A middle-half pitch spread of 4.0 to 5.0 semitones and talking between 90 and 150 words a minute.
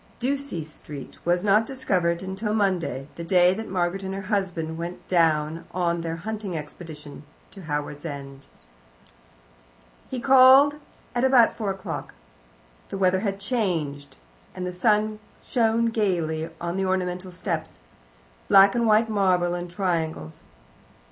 Yes: average, 4.3 semitones; average, 140 wpm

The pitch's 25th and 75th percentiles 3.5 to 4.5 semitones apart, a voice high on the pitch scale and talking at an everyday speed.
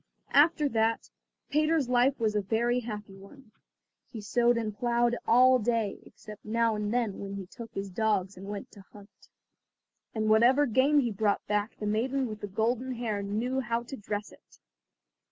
No: average, 2.9 semitones; high, 225 Hz; average, 175 wpm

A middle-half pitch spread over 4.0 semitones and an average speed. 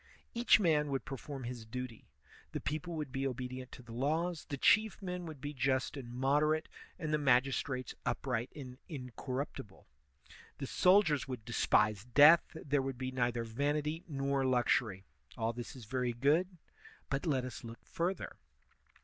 No: average, 3.4 semitones; average, 160 wpm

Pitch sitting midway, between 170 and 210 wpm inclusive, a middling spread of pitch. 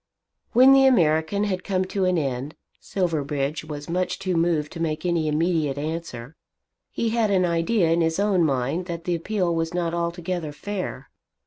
Yes: medium, 170 Hz; average, 175 wpm; average, 3.1 semitones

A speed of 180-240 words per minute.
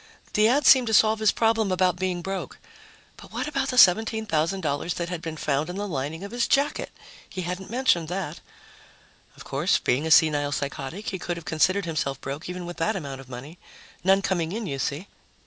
Yes: average, 200 wpm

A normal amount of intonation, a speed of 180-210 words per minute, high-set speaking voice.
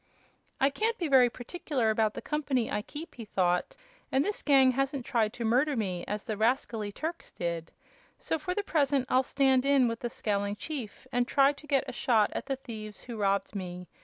Yes: average, 4.7 semitones; fast, 205 wpm; very high, 250 Hz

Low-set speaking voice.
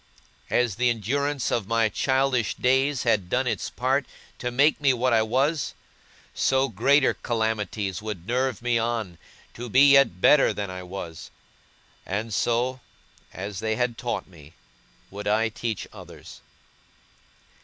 Yes: low, 115 Hz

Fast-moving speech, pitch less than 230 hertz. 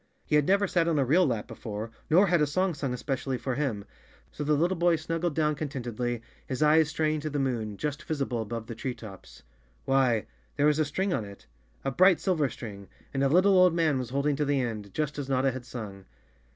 Yes: fast, 230 wpm; medium, 140 Hz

